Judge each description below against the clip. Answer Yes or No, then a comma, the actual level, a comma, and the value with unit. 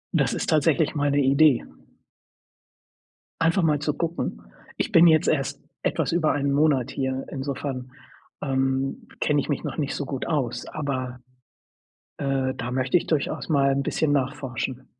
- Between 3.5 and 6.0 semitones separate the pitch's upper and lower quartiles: No, narrow, 2.4 semitones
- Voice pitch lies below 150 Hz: Yes, medium, 140 Hz